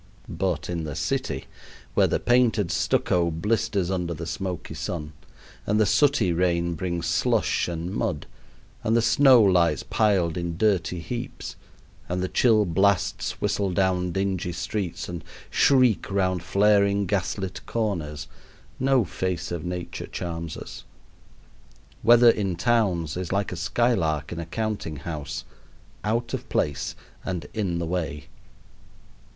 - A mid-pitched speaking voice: No, very low, 90 Hz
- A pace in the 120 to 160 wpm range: Yes, average, 140 wpm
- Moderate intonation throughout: Yes, average, 3.7 semitones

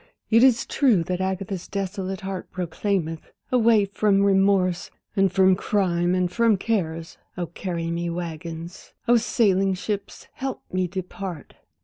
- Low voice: No, high, 190 Hz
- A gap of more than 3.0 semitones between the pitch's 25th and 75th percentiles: No, narrow, 2.5 semitones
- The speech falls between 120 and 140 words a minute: Yes, slow, 135 wpm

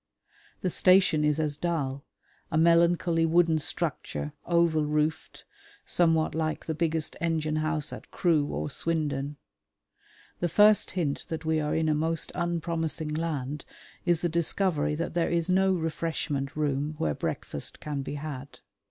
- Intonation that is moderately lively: No, narrow, 2.0 semitones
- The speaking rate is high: No, average, 145 wpm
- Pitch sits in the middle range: Yes, medium, 160 Hz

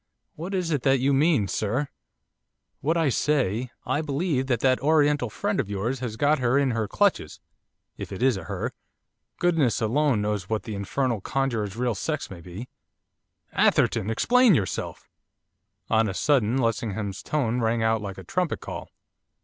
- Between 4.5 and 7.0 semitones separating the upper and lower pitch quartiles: Yes, average, 5.3 semitones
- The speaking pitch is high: No, low, 125 Hz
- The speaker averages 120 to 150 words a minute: No, average, 165 wpm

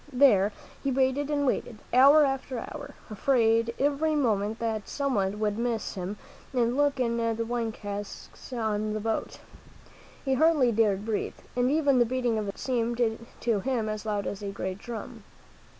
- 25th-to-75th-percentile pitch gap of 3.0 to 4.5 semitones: Yes, average, 3.7 semitones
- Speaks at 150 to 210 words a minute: Yes, average, 170 wpm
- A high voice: Yes, high, 230 Hz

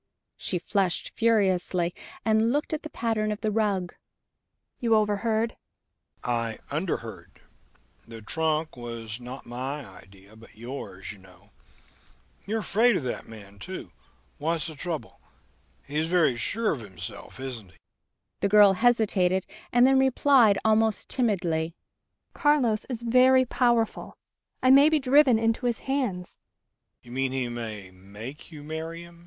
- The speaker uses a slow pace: Yes, slow, 125 wpm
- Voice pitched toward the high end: Yes, high, 195 Hz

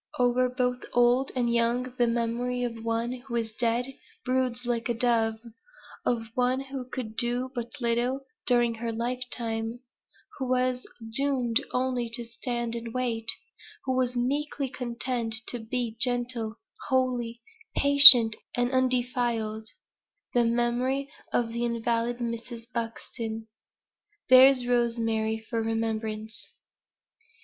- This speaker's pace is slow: Yes, slow, 120 wpm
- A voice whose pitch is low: No, high, 240 Hz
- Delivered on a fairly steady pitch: Yes, narrow, 1.6 semitones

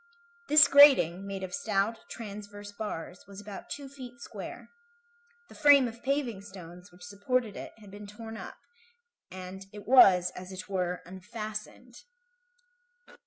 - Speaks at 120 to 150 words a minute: Yes, average, 140 wpm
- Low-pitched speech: No, high, 205 Hz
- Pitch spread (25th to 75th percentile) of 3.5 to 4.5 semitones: Yes, average, 4.1 semitones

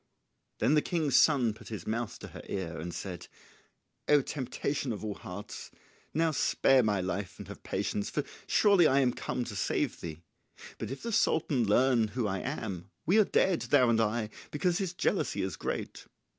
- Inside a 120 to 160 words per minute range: No, average, 185 wpm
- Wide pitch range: Yes, wide, 6.2 semitones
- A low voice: Yes, low, 120 Hz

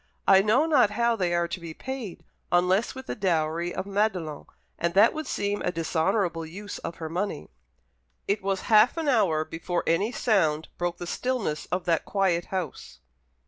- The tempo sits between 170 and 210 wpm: Yes, average, 180 wpm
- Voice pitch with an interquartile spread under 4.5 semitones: Yes, average, 4.0 semitones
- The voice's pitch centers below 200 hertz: Yes, medium, 185 Hz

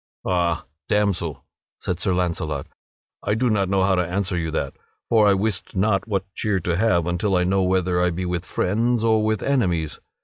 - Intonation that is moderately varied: Yes, average, 3.1 semitones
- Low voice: Yes, very low, 95 Hz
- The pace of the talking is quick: No, average, 195 wpm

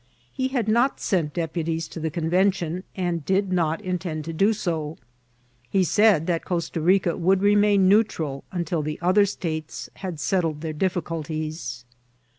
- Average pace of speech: Yes, average, 150 wpm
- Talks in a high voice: No, medium, 175 Hz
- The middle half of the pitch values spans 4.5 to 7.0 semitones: No, average, 3.4 semitones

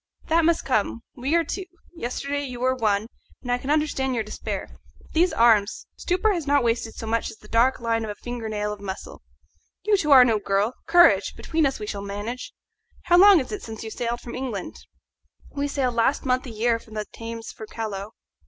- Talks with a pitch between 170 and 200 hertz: No, high, 240 Hz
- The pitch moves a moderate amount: Yes, average, 4.6 semitones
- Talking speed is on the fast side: Yes, fast, 215 wpm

